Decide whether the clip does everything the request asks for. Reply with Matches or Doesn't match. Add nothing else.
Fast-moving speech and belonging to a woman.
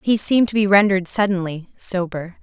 Doesn't match